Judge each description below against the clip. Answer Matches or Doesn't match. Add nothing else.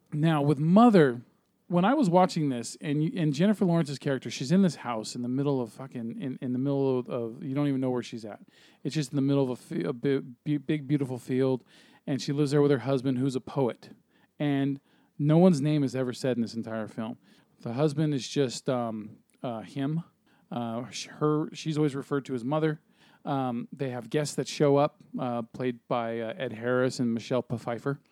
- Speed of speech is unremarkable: Doesn't match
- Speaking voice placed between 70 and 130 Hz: Doesn't match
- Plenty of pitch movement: Doesn't match